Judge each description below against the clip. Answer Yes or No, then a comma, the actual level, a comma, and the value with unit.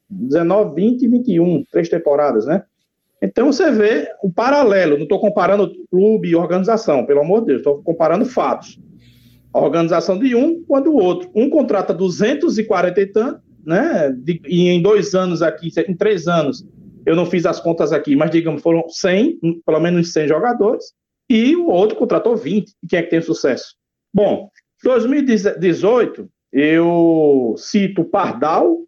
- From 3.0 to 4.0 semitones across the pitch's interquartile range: No, average, 4.8 semitones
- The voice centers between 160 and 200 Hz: Yes, medium, 185 Hz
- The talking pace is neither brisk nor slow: Yes, average, 160 wpm